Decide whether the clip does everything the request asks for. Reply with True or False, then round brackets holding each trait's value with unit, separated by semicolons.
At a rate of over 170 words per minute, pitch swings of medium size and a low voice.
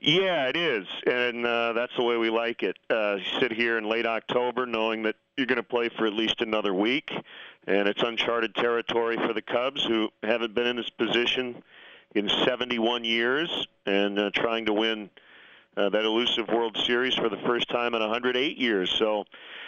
False (200 wpm; 1.4 semitones; 115 Hz)